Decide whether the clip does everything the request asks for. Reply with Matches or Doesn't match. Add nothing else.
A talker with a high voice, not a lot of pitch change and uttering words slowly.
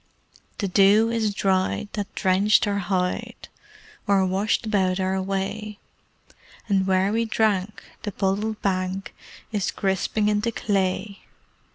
Matches